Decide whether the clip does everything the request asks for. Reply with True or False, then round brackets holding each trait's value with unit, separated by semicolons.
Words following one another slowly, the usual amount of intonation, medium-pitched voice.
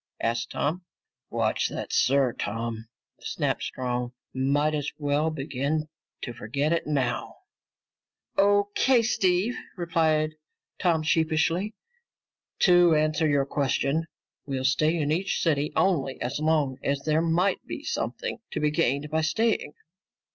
True (125 wpm; 3.5 semitones; 155 Hz)